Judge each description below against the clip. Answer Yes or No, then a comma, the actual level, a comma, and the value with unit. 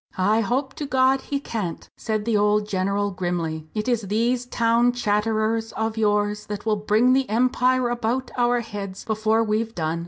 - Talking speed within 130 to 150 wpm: No, average, 175 wpm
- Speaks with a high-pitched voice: Yes, high, 220 Hz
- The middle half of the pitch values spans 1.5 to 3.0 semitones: Yes, average, 2.7 semitones